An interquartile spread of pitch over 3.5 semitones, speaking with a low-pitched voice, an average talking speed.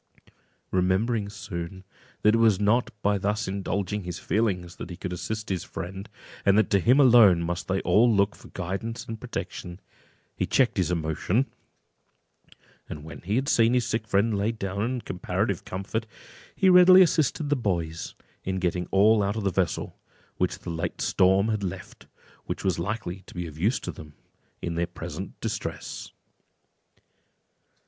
Yes: average, 3.9 semitones; low, 100 Hz; average, 170 wpm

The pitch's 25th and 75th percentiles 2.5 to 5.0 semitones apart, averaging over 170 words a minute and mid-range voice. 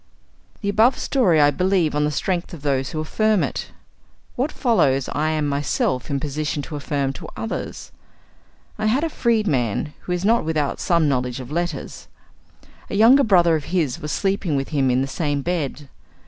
No: wide, 5.5 semitones; average, 185 wpm; medium, 155 Hz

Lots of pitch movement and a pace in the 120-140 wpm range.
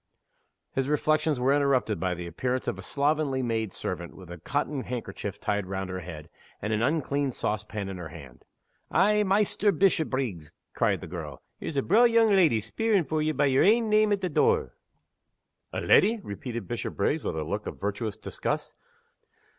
No: wide, 8.6 semitones; average, 180 wpm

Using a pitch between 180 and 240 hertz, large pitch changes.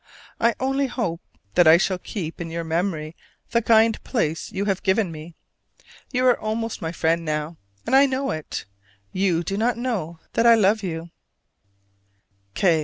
Yes: high, 190 Hz; wide, 5.8 semitones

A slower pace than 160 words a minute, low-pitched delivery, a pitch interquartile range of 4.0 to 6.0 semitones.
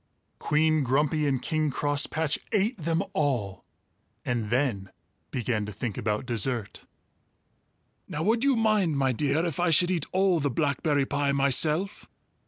No: average, 145 wpm; medium, 145 Hz; average, 4.4 semitones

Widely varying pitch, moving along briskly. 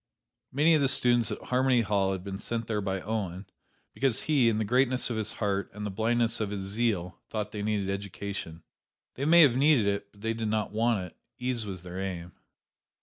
No: average, 3.5 semitones; fast, 210 wpm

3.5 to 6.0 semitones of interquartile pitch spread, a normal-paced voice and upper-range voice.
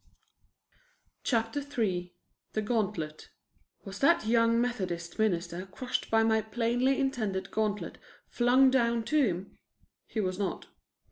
No: average, 4.1 semitones; slow, 120 wpm; high, 220 Hz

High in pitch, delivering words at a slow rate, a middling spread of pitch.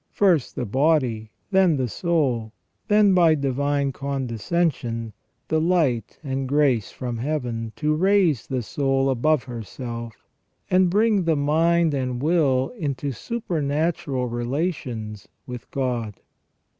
No: medium, 140 Hz; slow, 120 wpm; average, 5.0 semitones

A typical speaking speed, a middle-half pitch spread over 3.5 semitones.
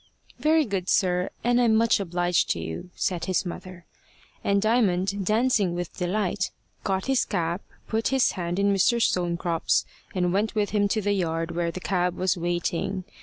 No: average, 170 wpm; average, 3.2 semitones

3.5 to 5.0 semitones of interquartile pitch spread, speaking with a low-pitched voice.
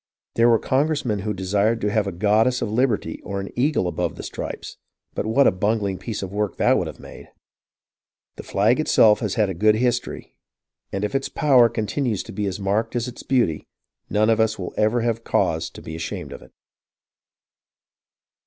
No: average, 3.1 semitones; low, 110 Hz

